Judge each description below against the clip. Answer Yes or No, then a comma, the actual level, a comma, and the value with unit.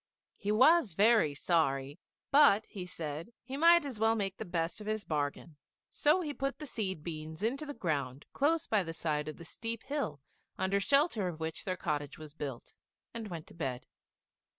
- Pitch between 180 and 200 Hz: Yes, high, 190 Hz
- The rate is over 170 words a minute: Yes, average, 190 wpm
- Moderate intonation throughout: No, wide, 7.4 semitones